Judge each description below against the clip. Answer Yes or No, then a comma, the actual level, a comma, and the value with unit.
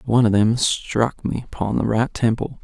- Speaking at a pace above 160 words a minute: Yes, fast, 205 wpm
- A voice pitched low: Yes, low, 115 Hz